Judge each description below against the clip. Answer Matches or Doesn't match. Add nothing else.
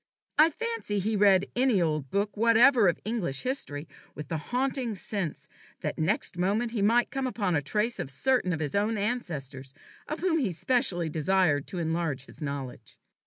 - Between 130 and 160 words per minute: Doesn't match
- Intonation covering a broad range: Matches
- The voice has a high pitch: Matches